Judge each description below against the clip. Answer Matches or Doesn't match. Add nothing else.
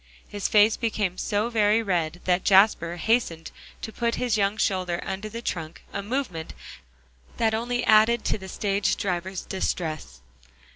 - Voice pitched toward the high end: Matches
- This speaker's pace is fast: Doesn't match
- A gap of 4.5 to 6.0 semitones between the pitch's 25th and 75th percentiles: Doesn't match